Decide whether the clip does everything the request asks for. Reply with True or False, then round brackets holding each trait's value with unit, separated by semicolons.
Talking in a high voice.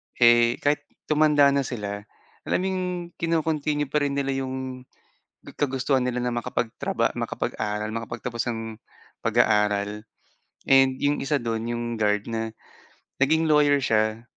False (125 Hz)